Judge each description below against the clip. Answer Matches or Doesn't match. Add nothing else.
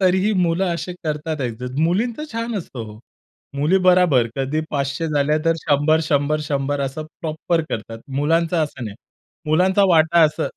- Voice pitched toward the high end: Doesn't match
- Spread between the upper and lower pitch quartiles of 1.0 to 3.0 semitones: Doesn't match